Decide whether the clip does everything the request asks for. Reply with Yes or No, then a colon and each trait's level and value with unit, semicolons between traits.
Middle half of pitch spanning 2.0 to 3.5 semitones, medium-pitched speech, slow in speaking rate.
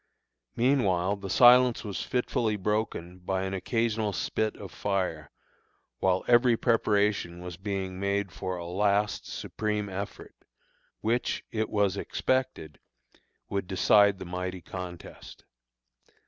No: average, 2.9 semitones; low, 100 Hz; slow, 120 wpm